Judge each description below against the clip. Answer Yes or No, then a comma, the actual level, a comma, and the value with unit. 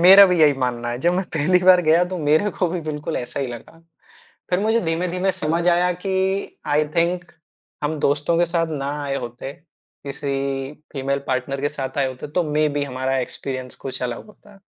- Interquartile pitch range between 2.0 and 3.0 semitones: No, average, 4.6 semitones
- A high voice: No, medium, 155 Hz